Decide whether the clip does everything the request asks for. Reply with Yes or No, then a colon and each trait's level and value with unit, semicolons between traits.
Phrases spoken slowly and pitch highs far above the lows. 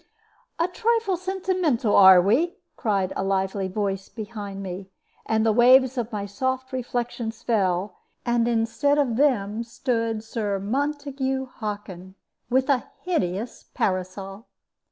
No: slow, 125 wpm; average, 5.0 semitones